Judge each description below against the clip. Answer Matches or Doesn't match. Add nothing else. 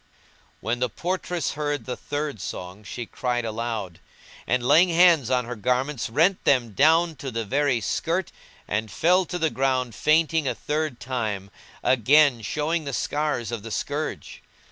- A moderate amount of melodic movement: Matches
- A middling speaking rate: Matches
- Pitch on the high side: Doesn't match